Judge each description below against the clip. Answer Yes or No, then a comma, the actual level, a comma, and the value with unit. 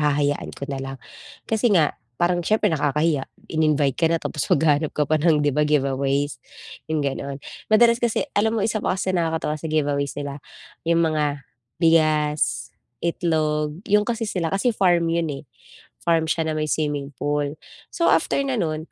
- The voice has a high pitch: No, medium, 155 Hz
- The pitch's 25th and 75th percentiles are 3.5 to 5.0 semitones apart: No, average, 2.7 semitones